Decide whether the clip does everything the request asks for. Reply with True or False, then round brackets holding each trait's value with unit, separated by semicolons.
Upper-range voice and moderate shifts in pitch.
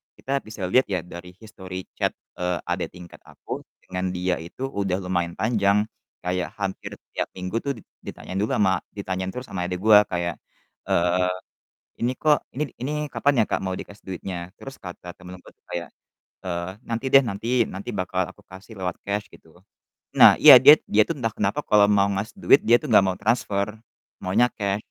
False (95 Hz; 3.3 semitones)